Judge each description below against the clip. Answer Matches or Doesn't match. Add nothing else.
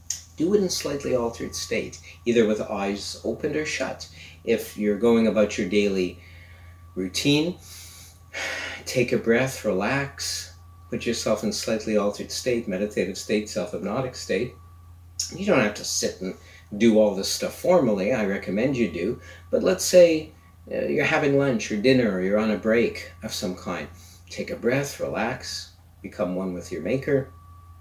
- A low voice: Matches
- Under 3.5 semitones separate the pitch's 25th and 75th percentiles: Doesn't match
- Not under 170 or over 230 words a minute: Doesn't match